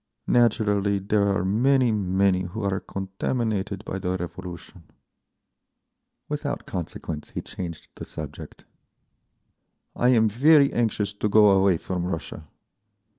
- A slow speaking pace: Yes, slow, 120 wpm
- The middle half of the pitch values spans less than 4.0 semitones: Yes, average, 2.9 semitones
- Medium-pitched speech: No, low, 100 Hz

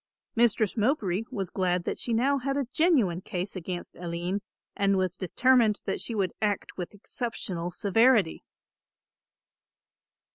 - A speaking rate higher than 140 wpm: No, slow, 135 wpm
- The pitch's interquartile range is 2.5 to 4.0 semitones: No, average, 4.7 semitones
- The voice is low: No, high, 200 Hz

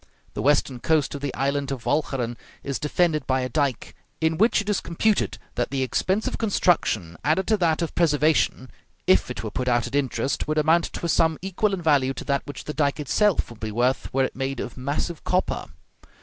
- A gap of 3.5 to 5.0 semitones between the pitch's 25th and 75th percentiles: Yes, average, 4.2 semitones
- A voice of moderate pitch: Yes, medium, 145 Hz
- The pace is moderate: No, fast, 215 wpm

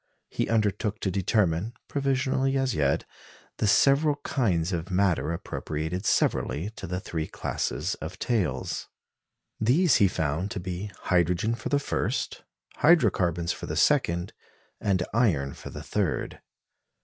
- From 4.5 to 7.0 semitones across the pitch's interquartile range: Yes, wide, 5.5 semitones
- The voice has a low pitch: Yes, very low, 95 Hz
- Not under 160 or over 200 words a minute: No, slow, 135 wpm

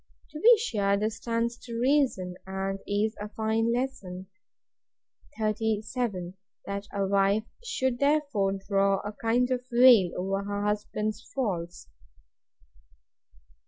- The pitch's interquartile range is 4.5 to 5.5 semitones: No, average, 3.3 semitones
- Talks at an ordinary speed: No, slow, 115 wpm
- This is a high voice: Yes, high, 215 Hz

